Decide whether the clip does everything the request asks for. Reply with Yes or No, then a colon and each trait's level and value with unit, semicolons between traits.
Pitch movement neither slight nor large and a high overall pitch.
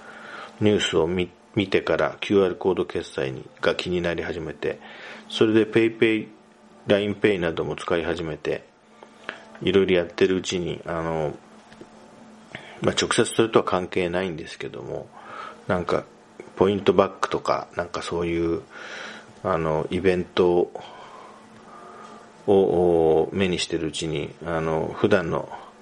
No: average, 3.1 semitones; very low, 90 Hz